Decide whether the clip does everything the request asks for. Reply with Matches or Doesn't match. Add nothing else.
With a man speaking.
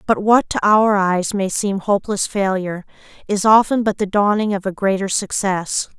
Doesn't match